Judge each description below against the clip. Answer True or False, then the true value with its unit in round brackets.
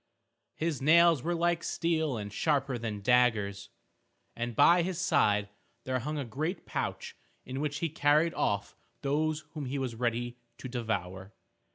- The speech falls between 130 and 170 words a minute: True (155 wpm)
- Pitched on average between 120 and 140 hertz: True (135 Hz)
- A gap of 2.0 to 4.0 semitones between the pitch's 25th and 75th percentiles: False (5.3 semitones)